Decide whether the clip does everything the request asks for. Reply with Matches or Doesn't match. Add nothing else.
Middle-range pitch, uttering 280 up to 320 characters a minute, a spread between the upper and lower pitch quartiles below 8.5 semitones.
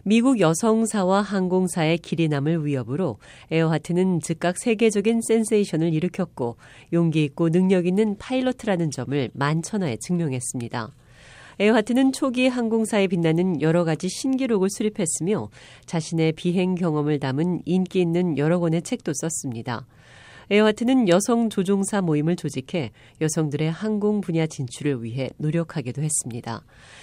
Doesn't match